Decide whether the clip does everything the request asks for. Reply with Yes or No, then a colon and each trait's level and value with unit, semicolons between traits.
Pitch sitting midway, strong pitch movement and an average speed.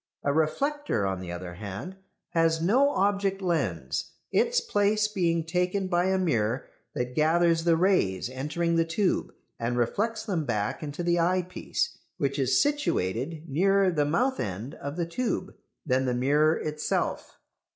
Yes: medium, 165 Hz; wide, 6.4 semitones; average, 150 wpm